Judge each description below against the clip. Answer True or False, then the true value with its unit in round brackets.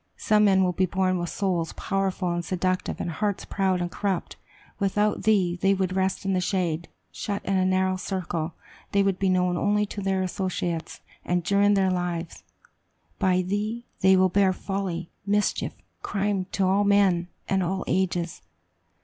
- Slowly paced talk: False (175 wpm)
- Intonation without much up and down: True (1.8 semitones)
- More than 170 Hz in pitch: True (190 Hz)